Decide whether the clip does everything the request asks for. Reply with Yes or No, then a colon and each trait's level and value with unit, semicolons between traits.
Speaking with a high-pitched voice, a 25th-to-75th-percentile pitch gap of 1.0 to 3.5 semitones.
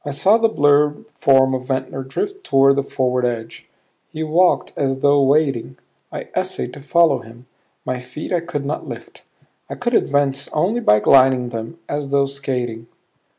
No: medium, 140 Hz; average, 2.7 semitones